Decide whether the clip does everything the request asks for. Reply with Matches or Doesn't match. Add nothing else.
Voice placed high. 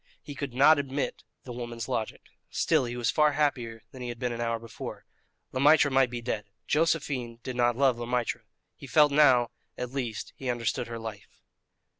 Doesn't match